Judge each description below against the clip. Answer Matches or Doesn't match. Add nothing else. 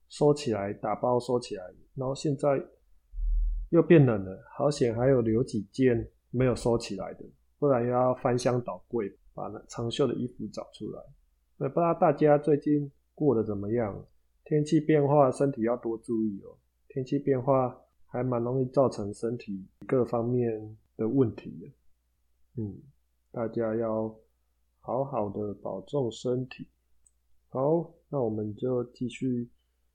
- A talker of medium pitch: Doesn't match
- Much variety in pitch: Doesn't match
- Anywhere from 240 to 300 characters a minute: Doesn't match